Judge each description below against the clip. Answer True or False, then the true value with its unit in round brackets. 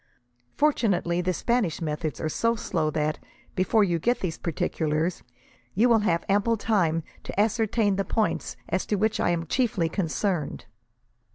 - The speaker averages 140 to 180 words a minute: True (155 wpm)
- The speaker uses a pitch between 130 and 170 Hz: False (185 Hz)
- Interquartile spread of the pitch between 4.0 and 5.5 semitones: True (4.9 semitones)